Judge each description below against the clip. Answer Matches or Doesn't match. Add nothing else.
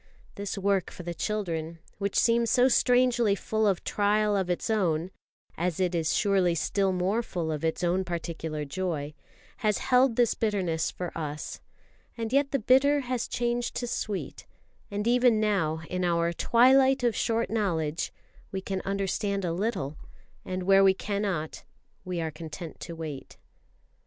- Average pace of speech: Matches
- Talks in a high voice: Matches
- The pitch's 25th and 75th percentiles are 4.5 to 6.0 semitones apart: Matches